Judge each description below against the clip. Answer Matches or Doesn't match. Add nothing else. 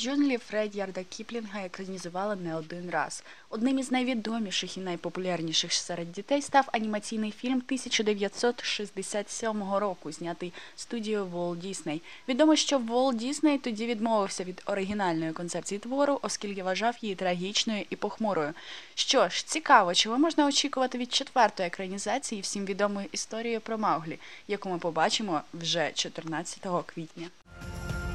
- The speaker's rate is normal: Matches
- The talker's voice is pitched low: Doesn't match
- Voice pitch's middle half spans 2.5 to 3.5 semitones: Doesn't match